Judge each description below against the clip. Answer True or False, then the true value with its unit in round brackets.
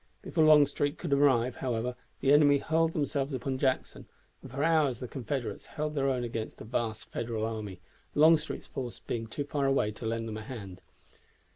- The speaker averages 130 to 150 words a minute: False (180 wpm)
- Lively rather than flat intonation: False (4.1 semitones)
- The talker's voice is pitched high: False (130 Hz)